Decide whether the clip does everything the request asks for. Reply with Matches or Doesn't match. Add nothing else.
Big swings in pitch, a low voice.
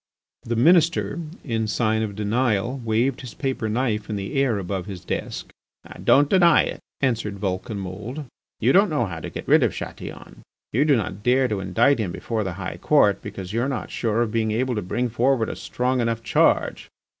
Doesn't match